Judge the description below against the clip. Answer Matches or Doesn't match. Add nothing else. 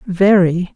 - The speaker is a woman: Matches